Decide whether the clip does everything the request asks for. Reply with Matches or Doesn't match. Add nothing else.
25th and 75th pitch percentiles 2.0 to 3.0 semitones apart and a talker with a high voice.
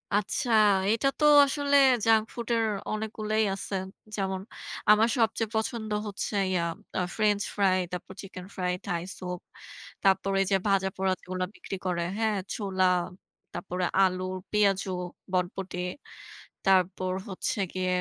Matches